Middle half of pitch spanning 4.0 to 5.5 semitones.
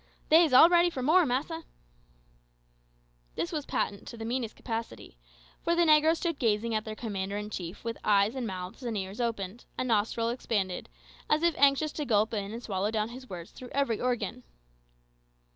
Yes: average, 5.1 semitones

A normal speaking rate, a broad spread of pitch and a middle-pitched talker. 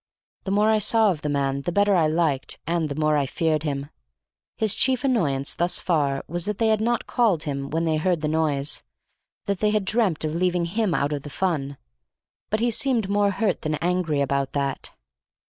No: fast, 210 wpm; wide, 5.7 semitones; medium, 170 Hz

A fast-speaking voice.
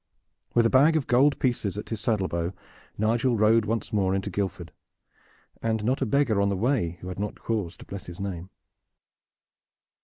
No: average, 185 wpm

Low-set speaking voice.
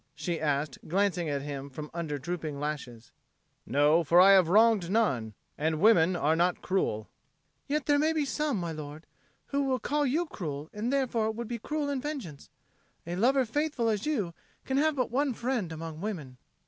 No: medium, 185 Hz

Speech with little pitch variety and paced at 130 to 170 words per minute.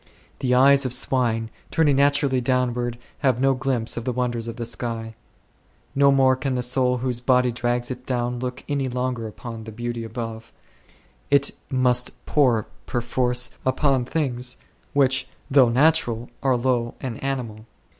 Yes: narrow, 1.8 semitones; average, 155 wpm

